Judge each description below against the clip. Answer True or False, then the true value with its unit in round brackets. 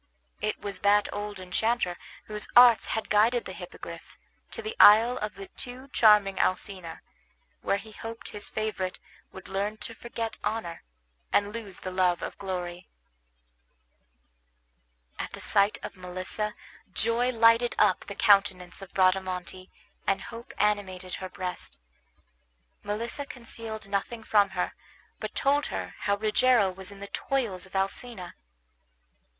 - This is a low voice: False (205 Hz)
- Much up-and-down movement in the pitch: False (3.3 semitones)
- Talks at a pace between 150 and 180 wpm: False (140 wpm)